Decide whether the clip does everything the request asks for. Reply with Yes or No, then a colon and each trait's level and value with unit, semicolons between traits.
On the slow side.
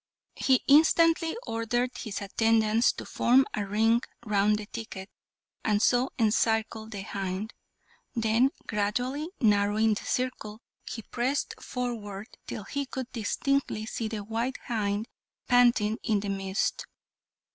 Yes: slow, 125 wpm